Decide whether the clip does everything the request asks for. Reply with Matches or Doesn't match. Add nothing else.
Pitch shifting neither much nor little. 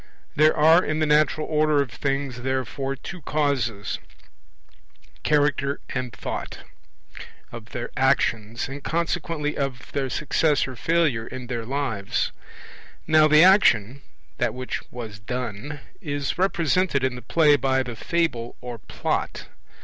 Matches